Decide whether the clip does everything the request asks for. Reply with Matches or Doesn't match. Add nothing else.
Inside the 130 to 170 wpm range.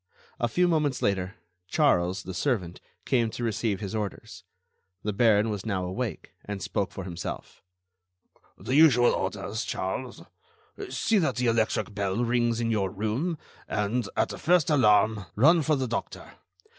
Matches